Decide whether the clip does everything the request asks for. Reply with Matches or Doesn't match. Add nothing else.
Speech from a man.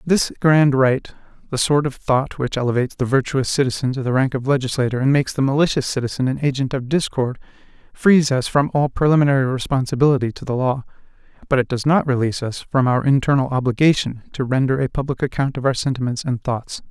Matches